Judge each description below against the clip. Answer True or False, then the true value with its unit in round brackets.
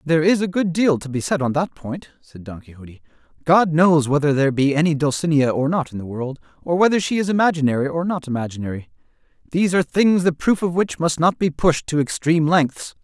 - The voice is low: False (155 Hz)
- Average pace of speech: False (220 wpm)